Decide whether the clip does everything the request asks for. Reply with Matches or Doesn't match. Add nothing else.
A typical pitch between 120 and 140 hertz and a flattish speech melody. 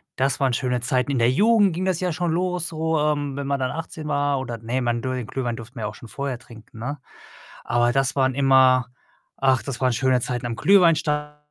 Doesn't match